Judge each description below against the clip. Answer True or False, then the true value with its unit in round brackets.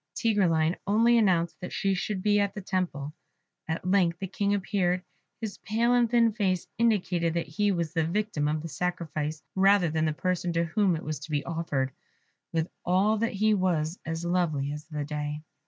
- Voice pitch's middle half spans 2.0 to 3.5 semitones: False (4.1 semitones)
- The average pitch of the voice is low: False (180 Hz)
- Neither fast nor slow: True (190 wpm)